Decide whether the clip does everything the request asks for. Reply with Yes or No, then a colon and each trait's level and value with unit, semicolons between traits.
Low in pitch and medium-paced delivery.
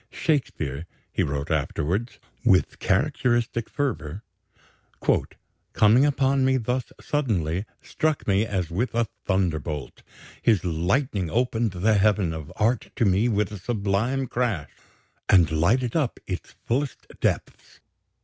No: low, 105 Hz; slow, 120 wpm